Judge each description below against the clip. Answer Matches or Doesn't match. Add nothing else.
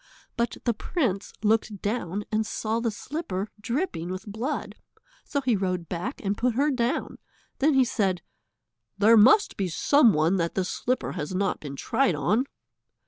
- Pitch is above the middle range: Matches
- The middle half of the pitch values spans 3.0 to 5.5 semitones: Matches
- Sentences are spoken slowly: Doesn't match